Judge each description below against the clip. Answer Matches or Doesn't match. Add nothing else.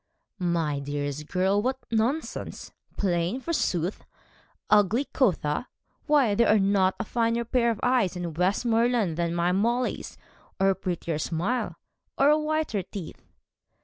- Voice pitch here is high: Matches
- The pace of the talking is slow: Matches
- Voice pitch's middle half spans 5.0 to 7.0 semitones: Matches